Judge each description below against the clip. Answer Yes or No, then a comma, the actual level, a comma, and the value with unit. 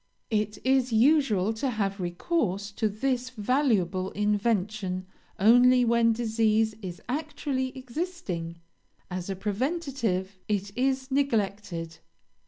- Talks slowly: Yes, slow, 105 wpm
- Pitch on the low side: No, high, 220 Hz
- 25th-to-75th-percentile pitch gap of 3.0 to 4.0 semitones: No, average, 4.7 semitones